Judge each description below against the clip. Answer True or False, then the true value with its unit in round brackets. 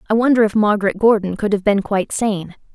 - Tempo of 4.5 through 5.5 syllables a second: False (6.3 syllables/s)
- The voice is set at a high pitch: True (210 Hz)